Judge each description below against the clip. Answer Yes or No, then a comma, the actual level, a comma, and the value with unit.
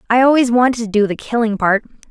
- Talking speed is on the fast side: Yes, fast, 230 wpm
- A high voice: Yes, high, 230 Hz